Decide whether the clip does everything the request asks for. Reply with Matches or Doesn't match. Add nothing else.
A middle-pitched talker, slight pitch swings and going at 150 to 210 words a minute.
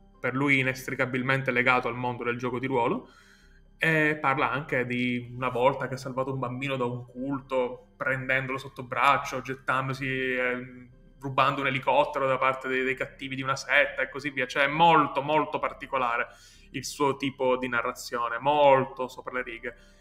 Doesn't match